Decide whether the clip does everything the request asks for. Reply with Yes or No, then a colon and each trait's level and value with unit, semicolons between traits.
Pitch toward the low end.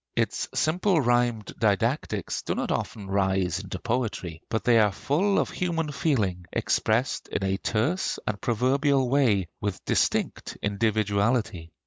Yes: low, 110 Hz